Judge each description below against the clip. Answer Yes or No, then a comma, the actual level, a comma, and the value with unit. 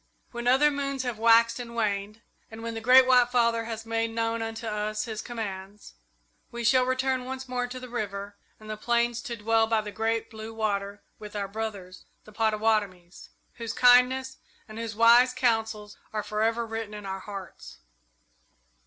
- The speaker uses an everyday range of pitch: No, narrow, 2.2 semitones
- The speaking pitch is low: No, high, 225 Hz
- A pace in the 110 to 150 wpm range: No, average, 175 wpm